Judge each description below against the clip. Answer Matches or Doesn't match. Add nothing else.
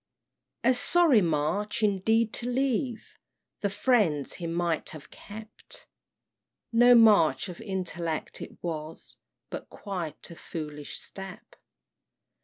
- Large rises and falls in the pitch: Matches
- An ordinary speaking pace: Doesn't match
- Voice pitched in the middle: Doesn't match